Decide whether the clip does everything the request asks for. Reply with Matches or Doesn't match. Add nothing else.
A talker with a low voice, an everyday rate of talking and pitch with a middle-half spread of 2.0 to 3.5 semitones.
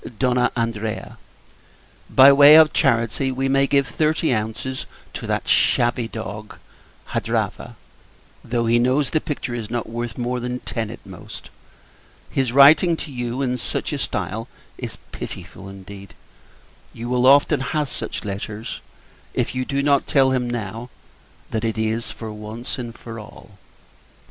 Matches